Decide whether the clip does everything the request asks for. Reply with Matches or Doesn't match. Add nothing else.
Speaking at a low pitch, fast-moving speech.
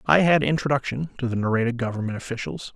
Doesn't match